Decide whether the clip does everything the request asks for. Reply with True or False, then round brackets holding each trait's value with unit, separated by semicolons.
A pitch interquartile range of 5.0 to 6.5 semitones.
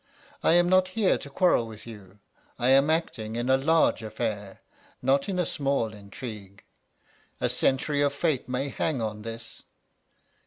True (5.3 semitones)